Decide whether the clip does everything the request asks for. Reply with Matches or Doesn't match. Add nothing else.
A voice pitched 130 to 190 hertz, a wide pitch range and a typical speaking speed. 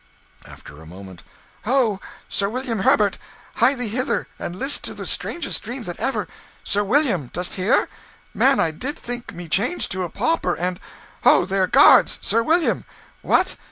Doesn't match